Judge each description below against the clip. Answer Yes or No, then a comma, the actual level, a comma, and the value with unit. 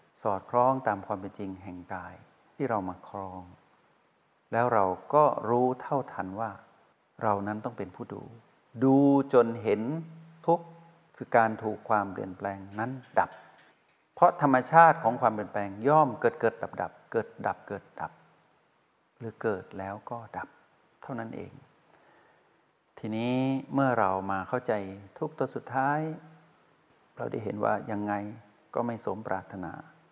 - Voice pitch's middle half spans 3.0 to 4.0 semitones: No, average, 5.3 semitones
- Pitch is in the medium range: No, low, 115 Hz